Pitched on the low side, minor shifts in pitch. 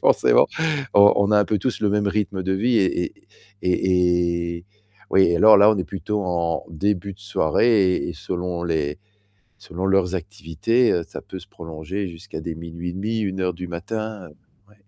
No: very low, 95 Hz; average, 3.1 semitones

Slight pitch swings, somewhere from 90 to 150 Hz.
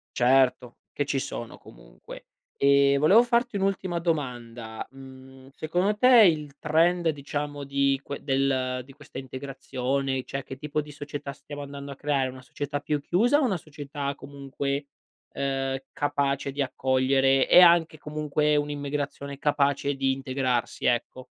Yes: narrow, 2.0 semitones; medium, 140 Hz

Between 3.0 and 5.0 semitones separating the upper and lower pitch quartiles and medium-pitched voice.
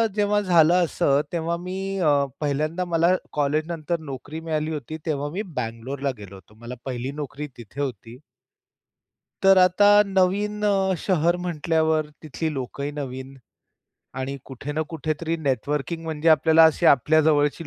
Yes: average, 3.5 semitones; medium, 155 Hz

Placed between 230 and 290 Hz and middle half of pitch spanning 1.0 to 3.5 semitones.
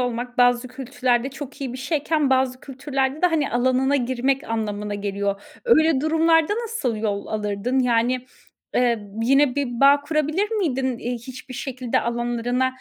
Yes: very high, 255 Hz; average, 2.9 semitones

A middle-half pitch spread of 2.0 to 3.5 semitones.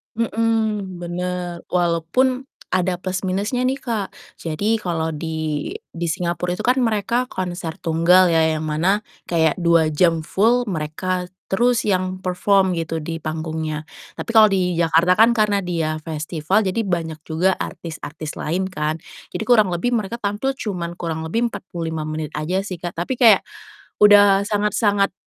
No: average, 4.1 semitones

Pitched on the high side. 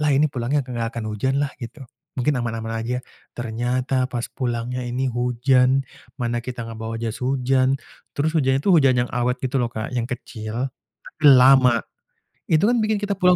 No: low, 125 Hz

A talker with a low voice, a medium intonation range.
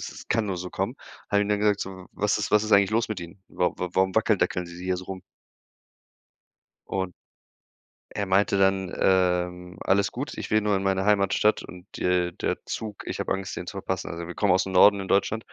No: very low, 95 Hz; narrow, 2.2 semitones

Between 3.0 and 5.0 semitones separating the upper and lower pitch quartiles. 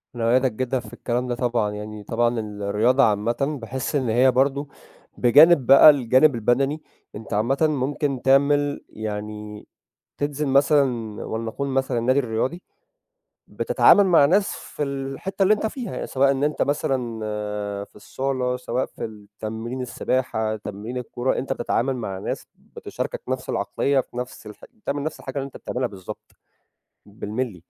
Yes: average, 3.7 semitones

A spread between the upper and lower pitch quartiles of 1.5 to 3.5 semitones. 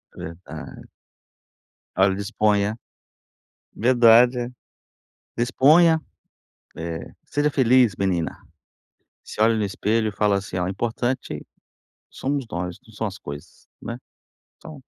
No: average, 4.2 semitones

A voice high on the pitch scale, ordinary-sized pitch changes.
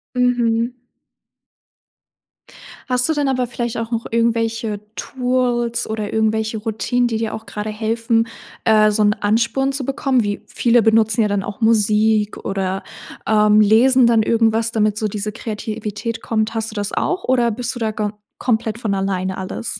No: high, 225 Hz; narrow, 2.0 semitones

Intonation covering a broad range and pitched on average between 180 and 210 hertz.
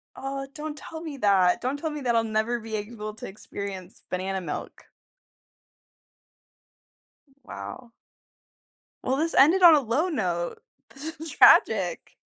No: wide, 6.5 semitones; high, 240 Hz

